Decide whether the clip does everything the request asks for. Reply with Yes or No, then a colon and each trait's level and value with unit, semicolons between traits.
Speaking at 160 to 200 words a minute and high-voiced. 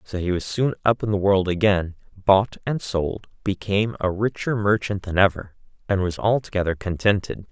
No: average, 175 wpm; low, 100 Hz